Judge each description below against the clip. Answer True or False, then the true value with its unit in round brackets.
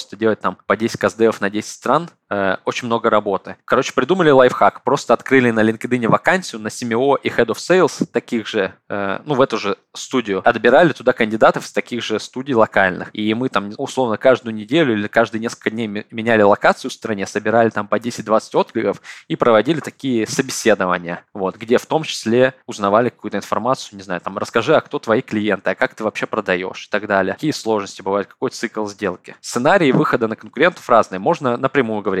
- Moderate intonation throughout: True (3.0 semitones)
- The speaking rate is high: True (190 wpm)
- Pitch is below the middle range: True (110 Hz)